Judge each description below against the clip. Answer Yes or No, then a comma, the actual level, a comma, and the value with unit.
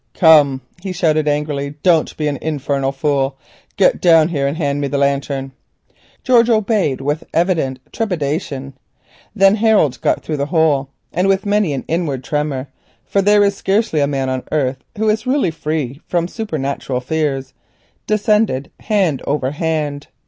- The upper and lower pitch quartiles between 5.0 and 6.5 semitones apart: Yes, wide, 5.5 semitones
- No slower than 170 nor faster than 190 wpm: No, average, 155 wpm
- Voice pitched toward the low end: No, medium, 150 Hz